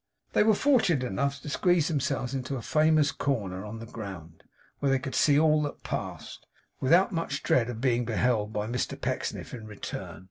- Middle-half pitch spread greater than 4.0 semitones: Yes, average, 5.2 semitones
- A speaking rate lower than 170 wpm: No, average, 185 wpm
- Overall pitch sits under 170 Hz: Yes, low, 135 Hz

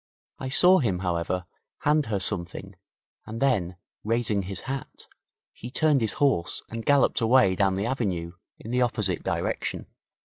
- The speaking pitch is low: Yes, low, 110 Hz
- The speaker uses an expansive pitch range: Yes, wide, 5.8 semitones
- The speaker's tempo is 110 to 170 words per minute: Yes, average, 150 wpm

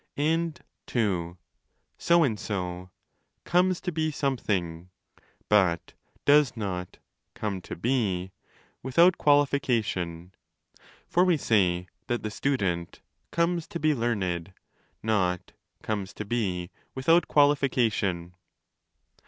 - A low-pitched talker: Yes, low, 110 Hz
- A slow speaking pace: Yes, slow, 110 wpm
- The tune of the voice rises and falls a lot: Yes, wide, 8.1 semitones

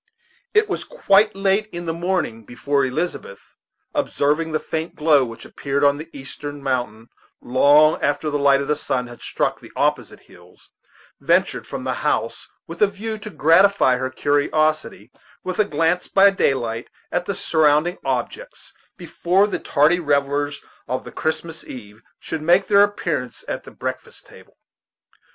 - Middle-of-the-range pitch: Yes, medium, 155 Hz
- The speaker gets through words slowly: No, average, 160 wpm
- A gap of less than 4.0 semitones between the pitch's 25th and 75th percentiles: No, average, 4.5 semitones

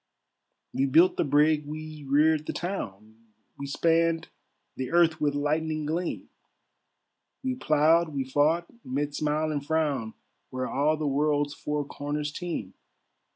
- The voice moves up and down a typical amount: No, narrow, 1.9 semitones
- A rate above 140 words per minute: No, slow, 135 wpm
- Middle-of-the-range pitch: Yes, medium, 150 Hz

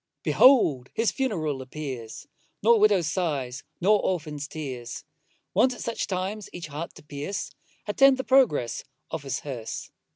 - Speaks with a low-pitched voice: No, medium, 155 Hz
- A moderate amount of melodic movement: No, wide, 7.3 semitones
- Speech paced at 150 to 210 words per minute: No, average, 140 wpm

